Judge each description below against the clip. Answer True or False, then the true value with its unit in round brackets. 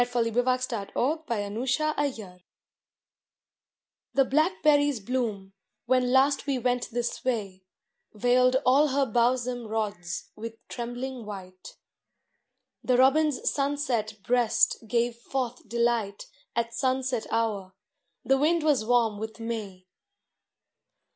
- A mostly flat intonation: False (3.1 semitones)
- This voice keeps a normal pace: False (120 wpm)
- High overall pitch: True (245 Hz)